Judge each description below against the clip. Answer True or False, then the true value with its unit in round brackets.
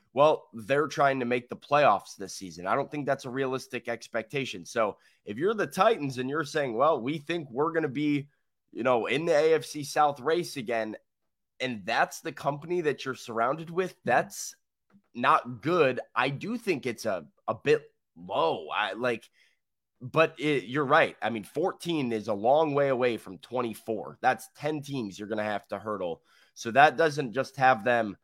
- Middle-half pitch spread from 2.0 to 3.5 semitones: False (4.6 semitones)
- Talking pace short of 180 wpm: False (190 wpm)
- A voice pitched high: False (135 Hz)